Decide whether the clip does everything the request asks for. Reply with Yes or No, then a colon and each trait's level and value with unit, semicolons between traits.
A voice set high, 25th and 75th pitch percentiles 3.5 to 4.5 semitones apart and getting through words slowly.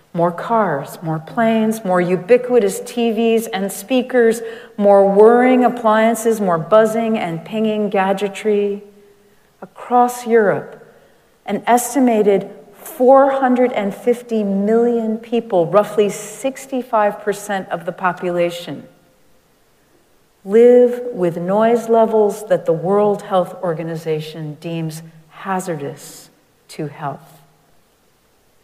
Yes: high, 210 Hz; average, 3.8 semitones; slow, 90 wpm